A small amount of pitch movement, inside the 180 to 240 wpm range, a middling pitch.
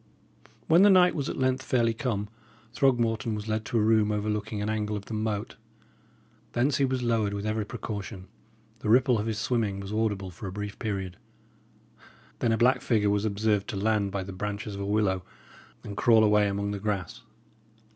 No: narrow, 2.1 semitones; average, 195 wpm; low, 105 Hz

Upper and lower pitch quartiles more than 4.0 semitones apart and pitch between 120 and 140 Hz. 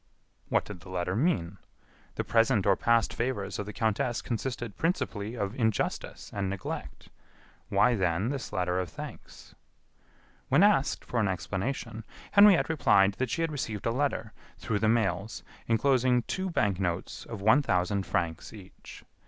No: average, 4.7 semitones; low, 110 Hz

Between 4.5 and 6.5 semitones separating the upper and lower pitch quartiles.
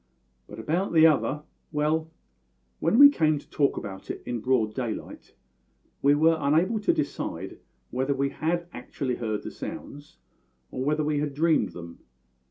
No: average, 3.9 semitones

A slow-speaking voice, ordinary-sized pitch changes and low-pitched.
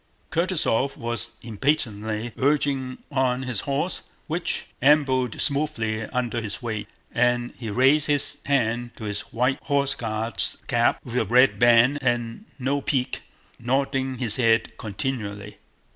Yes: slow, 130 wpm; average, 3.2 semitones; low, 125 Hz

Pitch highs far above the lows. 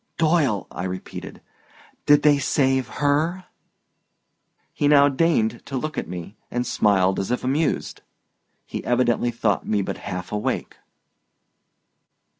Yes: wide, 5.8 semitones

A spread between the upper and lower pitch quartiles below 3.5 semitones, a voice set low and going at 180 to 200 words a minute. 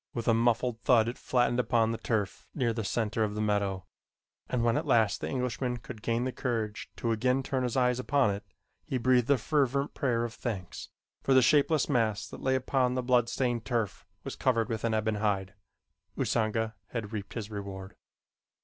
Yes: narrow, 2.6 semitones; low, 115 Hz; average, 195 wpm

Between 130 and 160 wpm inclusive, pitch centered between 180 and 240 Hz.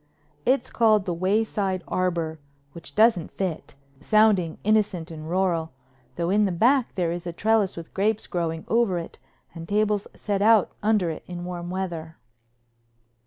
Yes: average, 155 wpm; medium, 185 Hz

